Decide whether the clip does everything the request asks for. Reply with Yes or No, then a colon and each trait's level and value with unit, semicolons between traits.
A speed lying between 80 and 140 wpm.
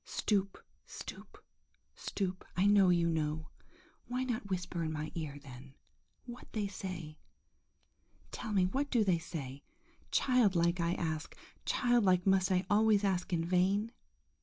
Yes: slow, 135 wpm